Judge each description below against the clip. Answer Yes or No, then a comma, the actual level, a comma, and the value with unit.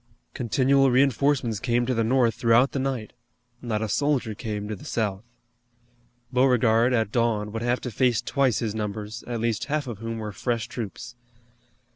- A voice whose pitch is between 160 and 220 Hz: No, low, 115 Hz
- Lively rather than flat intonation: No, average, 2.7 semitones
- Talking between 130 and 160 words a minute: No, average, 170 wpm